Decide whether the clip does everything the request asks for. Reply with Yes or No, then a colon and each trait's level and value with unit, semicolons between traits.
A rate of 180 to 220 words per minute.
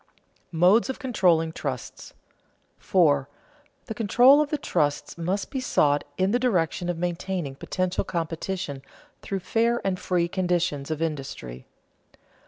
No: slow, 135 wpm